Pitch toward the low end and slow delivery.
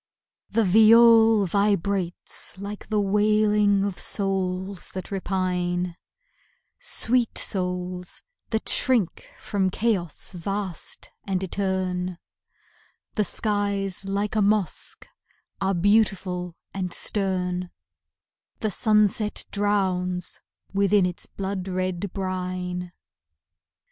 No: high, 195 Hz; slow, 90 wpm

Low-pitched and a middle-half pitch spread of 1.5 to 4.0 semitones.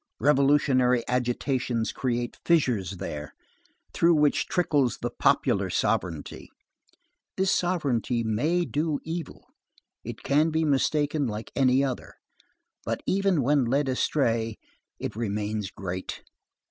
No: low, 130 Hz; average, 4.6 semitones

